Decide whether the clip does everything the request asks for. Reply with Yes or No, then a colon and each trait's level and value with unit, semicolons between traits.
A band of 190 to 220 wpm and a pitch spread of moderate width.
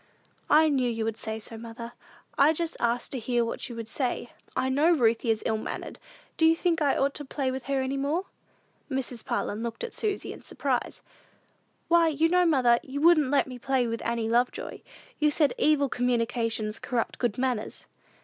Yes: average, 195 wpm; average, 4.1 semitones